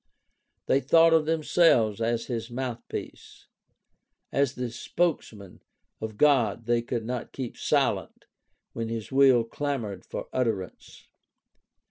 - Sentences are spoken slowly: Yes, slow, 115 wpm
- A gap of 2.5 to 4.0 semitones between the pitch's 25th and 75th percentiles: Yes, average, 3.5 semitones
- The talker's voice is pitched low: Yes, low, 120 Hz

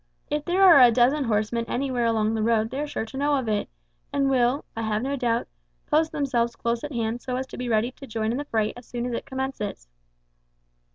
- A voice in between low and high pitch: No, high, 245 Hz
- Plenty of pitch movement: No, average, 3.3 semitones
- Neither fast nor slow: No, fast, 235 wpm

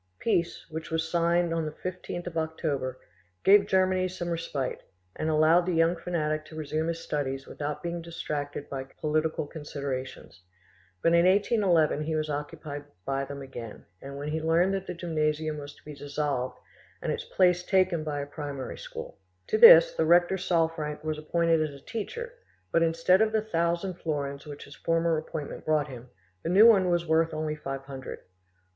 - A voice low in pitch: No, medium, 160 Hz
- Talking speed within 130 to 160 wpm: No, average, 175 wpm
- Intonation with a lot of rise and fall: No, average, 3.0 semitones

